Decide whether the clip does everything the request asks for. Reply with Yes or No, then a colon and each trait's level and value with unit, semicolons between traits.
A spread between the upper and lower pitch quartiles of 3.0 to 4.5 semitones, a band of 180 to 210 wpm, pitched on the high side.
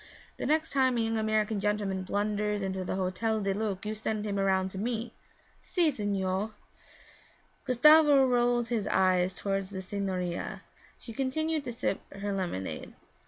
No: average, 3.9 semitones; average, 155 wpm; high, 210 Hz